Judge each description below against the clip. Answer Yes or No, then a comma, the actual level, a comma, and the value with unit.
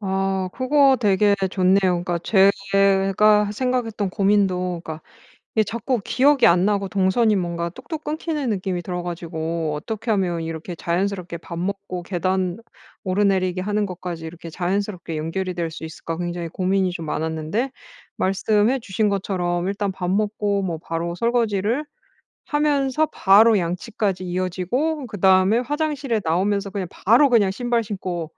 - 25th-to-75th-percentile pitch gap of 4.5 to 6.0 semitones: No, average, 3.4 semitones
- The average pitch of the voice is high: Yes, high, 195 Hz